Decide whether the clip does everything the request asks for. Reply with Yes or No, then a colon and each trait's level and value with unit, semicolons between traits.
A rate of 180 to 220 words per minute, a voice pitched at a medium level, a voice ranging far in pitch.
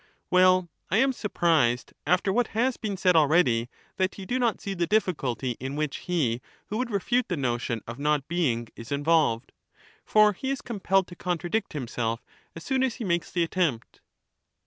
Yes: average, 185 wpm; medium, 175 Hz; wide, 7.2 semitones